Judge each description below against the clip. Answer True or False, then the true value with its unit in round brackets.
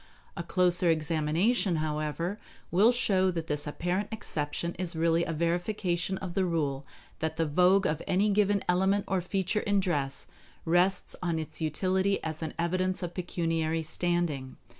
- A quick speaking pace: False (155 wpm)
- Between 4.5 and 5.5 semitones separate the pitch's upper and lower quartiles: False (2.9 semitones)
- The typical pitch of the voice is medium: True (175 Hz)